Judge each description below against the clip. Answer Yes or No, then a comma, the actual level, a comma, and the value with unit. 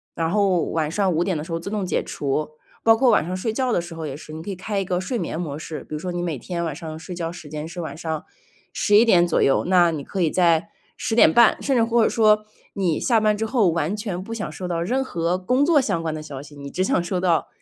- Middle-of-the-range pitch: Yes, medium, 175 Hz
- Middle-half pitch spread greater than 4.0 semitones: Yes, average, 4.6 semitones